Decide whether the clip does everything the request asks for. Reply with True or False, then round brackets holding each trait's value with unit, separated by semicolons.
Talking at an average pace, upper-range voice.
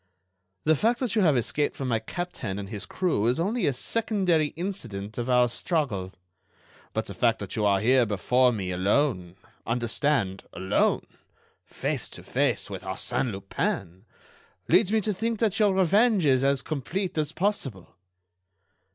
False (150 wpm; 135 Hz)